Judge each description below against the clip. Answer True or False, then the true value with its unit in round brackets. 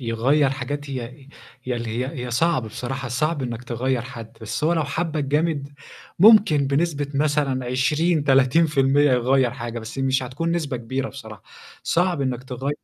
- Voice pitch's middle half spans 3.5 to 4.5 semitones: False (3.1 semitones)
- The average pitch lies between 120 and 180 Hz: True (135 Hz)